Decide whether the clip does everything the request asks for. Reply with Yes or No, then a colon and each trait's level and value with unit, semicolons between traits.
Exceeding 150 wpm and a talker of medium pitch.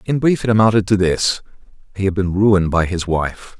No: average, 200 wpm; low, 100 Hz